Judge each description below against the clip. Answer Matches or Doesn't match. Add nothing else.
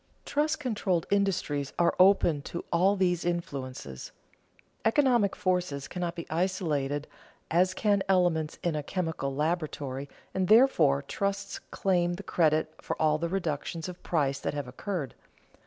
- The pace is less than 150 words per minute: Matches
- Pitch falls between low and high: Matches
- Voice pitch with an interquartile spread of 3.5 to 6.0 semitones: Matches